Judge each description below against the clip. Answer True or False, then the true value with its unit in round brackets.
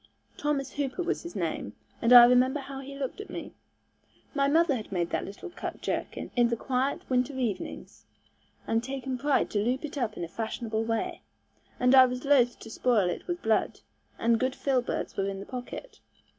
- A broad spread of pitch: False (3.4 semitones)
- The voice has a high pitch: True (250 Hz)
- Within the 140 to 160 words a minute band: False (195 wpm)